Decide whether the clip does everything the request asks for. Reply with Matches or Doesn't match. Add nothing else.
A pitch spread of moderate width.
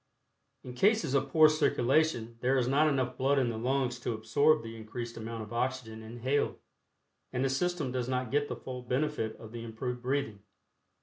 Matches